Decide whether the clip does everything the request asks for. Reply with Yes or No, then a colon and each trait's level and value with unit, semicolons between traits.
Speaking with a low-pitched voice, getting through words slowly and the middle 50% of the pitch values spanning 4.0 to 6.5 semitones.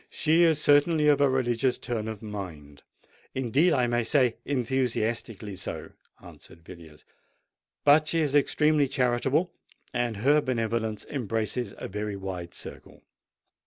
Yes: low, 120 Hz; slow, 125 wpm; average, 5.1 semitones